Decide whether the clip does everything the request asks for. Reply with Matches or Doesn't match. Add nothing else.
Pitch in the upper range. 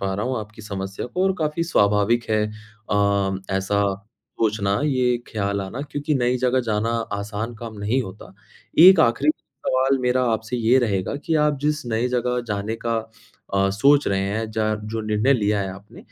Doesn't match